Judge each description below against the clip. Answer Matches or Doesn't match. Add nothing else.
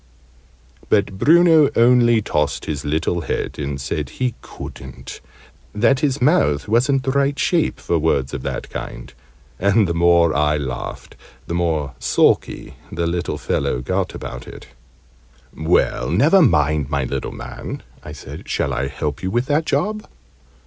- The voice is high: Doesn't match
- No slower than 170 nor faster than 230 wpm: Doesn't match